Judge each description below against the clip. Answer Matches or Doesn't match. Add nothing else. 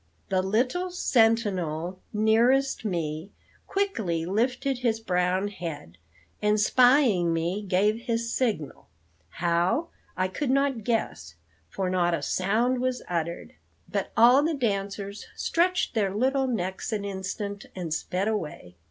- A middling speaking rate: Doesn't match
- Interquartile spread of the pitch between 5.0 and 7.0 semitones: Matches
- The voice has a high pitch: Matches